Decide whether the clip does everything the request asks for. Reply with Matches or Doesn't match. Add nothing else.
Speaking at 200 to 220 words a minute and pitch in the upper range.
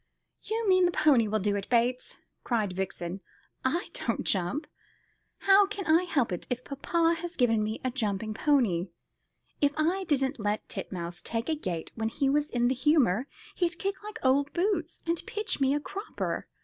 Doesn't match